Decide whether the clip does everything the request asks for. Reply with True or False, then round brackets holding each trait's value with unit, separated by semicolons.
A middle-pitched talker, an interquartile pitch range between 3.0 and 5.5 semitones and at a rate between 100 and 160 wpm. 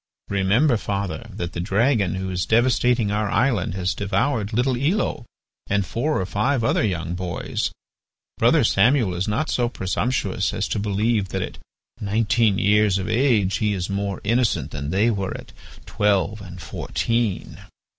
False (105 Hz; 3.7 semitones; 155 wpm)